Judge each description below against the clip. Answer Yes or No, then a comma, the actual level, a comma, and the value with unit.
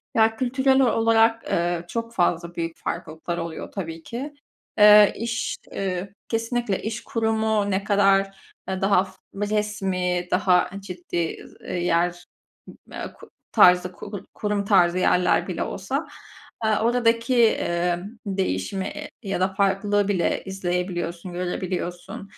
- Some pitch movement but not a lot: Yes, average, 3.7 semitones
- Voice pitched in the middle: No, high, 195 Hz